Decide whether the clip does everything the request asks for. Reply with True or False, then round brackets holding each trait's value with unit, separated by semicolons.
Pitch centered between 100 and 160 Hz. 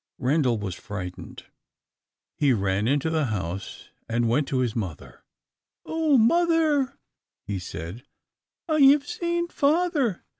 True (140 Hz)